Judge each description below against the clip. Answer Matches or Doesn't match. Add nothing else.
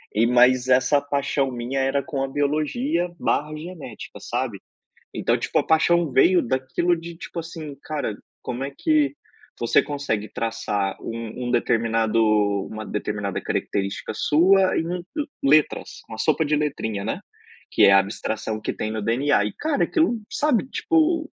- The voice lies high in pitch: Doesn't match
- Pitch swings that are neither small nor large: Doesn't match